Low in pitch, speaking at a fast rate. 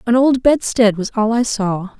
No: high, 225 Hz; fast, 210 wpm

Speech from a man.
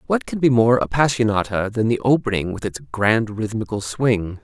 Yes: male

